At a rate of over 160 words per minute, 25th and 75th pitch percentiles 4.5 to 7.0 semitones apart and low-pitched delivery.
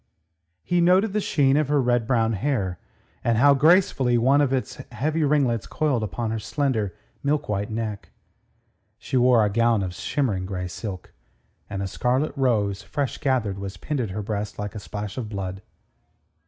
Yes: average, 175 wpm; average, 5.3 semitones; low, 115 Hz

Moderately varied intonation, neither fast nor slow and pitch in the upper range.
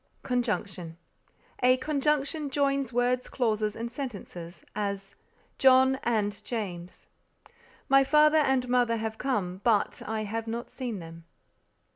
No: average, 4.4 semitones; slow, 120 wpm; high, 235 Hz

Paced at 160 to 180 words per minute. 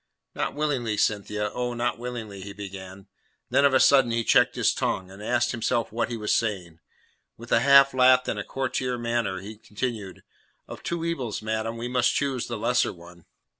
No: average, 190 wpm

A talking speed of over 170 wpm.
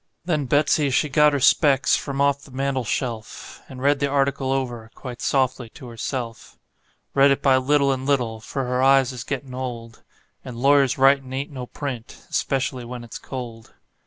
Yes: average, 180 wpm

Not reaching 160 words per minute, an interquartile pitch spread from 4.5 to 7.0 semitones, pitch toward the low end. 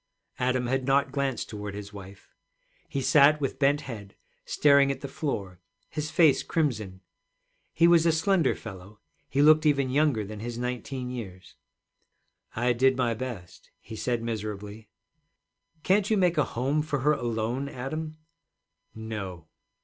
Yes: average, 150 wpm; average, 5.1 semitones; low, 130 Hz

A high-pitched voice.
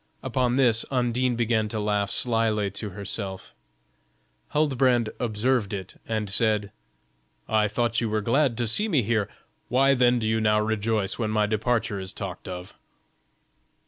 No: low, 110 Hz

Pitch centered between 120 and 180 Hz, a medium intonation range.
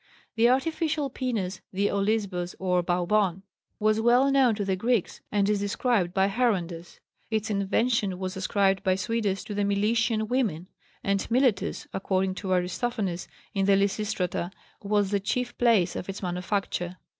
No: high, 200 Hz; average, 3.3 semitones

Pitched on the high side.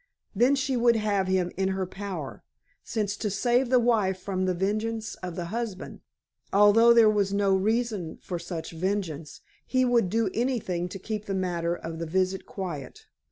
Yes: high, 195 Hz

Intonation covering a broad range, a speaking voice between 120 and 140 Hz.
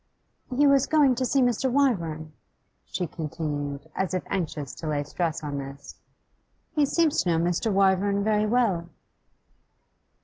No: wide, 7.9 semitones; medium, 185 Hz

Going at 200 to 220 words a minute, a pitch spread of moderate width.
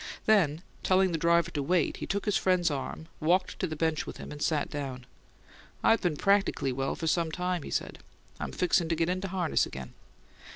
Yes: fast, 205 wpm; average, 3.5 semitones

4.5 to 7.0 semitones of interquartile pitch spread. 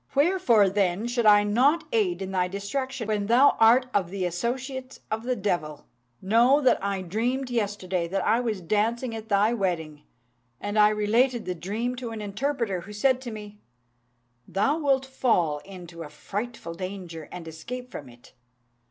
Yes: average, 4.9 semitones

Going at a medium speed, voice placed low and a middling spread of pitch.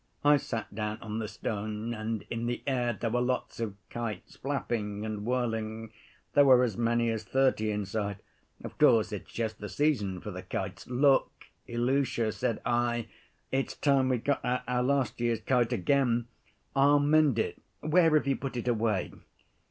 Yes: average, 175 wpm; low, 120 Hz; average, 3.2 semitones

